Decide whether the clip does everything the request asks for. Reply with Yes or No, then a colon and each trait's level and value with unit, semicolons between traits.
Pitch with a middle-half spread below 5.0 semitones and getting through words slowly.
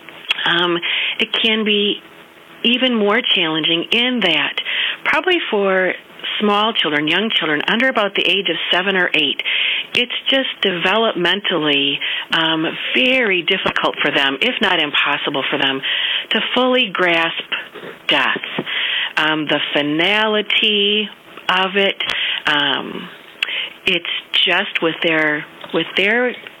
No: wide, 5.6 semitones; slow, 115 wpm